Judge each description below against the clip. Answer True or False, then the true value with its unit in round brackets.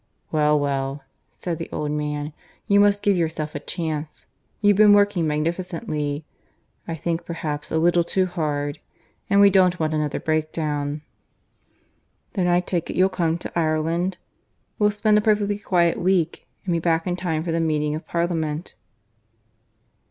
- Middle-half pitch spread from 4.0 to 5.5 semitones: False (3.3 semitones)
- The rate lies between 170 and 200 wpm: False (155 wpm)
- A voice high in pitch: False (165 Hz)